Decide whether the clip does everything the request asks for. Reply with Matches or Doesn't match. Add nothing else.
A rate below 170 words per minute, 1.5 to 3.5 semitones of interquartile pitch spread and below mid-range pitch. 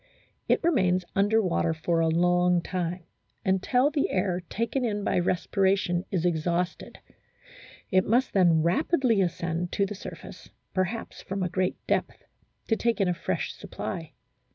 Doesn't match